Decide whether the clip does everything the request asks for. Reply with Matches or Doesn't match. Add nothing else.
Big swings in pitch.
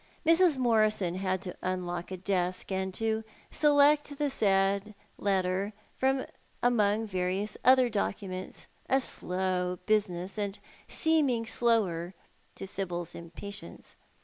Doesn't match